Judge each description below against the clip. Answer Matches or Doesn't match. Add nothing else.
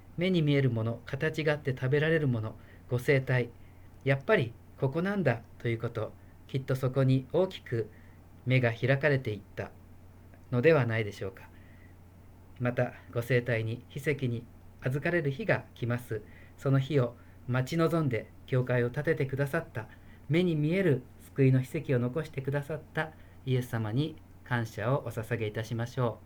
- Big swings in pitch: Doesn't match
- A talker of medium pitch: Doesn't match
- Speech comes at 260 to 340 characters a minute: Matches